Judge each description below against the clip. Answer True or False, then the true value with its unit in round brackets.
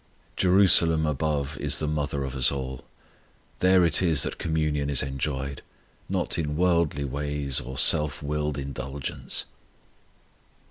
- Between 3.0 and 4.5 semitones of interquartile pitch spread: False (2.5 semitones)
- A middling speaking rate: False (130 wpm)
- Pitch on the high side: False (75 Hz)